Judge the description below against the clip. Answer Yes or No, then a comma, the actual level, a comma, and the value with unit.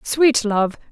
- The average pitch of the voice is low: No, high, 235 Hz